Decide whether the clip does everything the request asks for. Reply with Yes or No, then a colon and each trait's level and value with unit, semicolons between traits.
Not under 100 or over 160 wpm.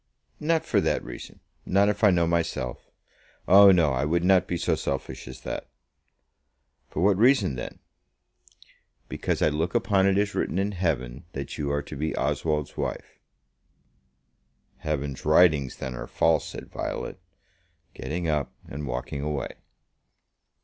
Yes: average, 150 wpm